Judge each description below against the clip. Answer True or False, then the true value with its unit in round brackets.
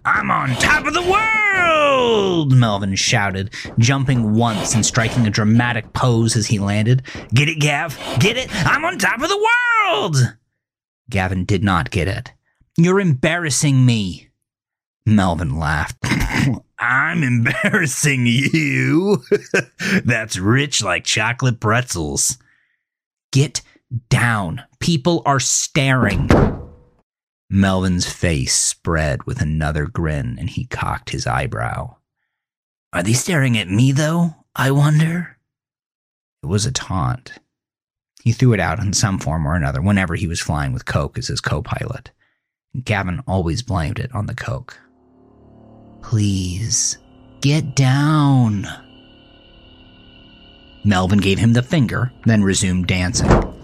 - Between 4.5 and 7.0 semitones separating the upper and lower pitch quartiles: True (5.4 semitones)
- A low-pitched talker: True (125 Hz)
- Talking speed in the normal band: False (125 wpm)